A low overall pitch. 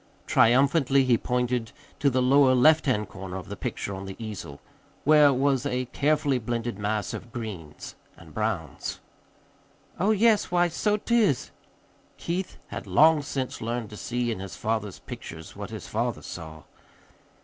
Yes: low, 125 Hz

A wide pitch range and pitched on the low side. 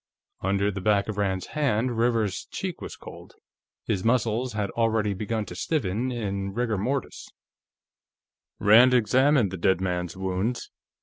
No: average, 3.7 semitones; low, 105 Hz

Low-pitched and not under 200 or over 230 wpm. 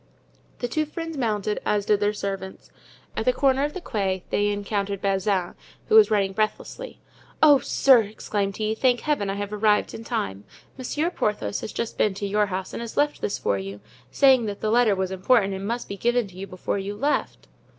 No: high, 210 Hz; fast, 205 wpm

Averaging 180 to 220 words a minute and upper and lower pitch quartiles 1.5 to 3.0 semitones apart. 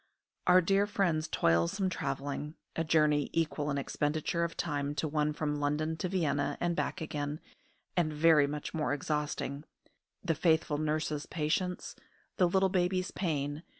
No: average, 150 wpm; narrow, 2.6 semitones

